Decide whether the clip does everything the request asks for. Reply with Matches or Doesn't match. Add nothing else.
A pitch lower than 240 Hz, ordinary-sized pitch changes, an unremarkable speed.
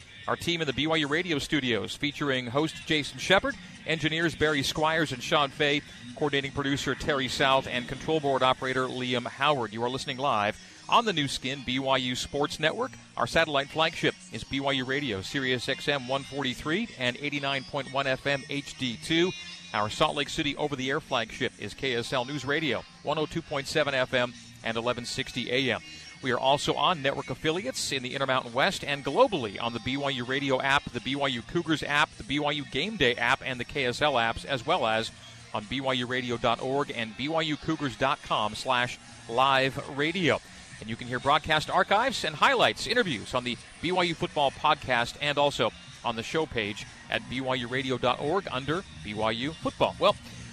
Matches